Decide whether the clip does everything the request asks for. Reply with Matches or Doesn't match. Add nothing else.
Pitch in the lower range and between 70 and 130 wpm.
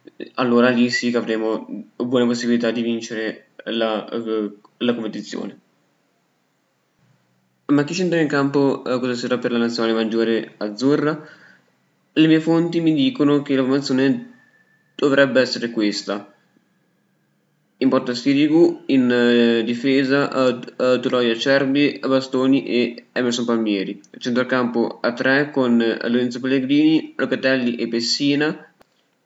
Matches